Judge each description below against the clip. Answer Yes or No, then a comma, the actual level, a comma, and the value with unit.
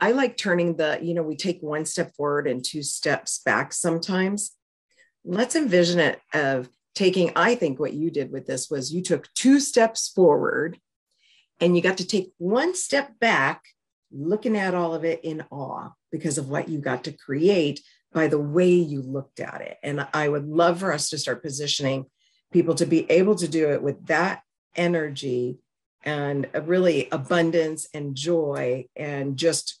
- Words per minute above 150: Yes, average, 180 wpm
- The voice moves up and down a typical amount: Yes, average, 3.7 semitones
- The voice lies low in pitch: No, medium, 165 Hz